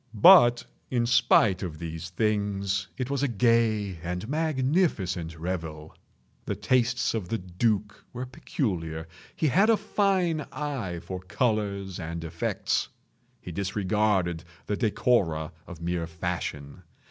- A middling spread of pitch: No, wide, 5.9 semitones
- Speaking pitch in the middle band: No, low, 100 Hz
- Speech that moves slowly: Yes, slow, 125 wpm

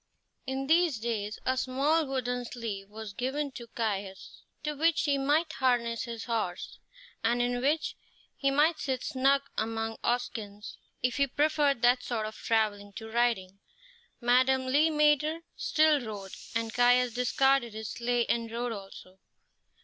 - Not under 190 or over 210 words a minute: No, average, 150 wpm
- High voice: Yes, high, 245 Hz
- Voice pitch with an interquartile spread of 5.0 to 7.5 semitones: No, average, 3.7 semitones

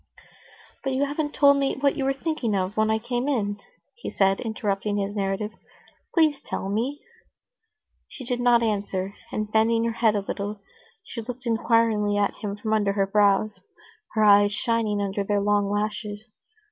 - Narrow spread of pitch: No, average, 3.0 semitones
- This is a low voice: No, high, 215 Hz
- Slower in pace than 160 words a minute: No, average, 170 wpm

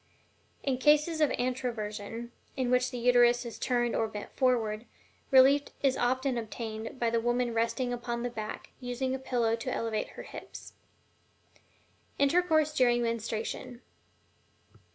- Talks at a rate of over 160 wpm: No, slow, 135 wpm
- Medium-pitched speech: No, high, 245 Hz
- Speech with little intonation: Yes, narrow, 2.1 semitones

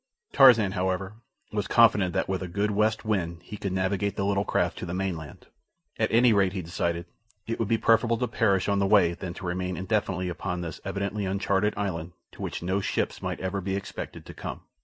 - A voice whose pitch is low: Yes, very low, 95 Hz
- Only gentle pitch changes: Yes, narrow, 2.3 semitones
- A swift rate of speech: Yes, fast, 210 wpm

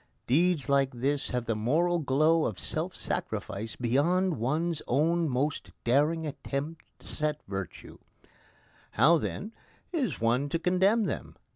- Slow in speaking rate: Yes, slow, 130 wpm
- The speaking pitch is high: No, medium, 150 Hz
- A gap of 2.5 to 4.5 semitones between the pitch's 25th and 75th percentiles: No, average, 5.1 semitones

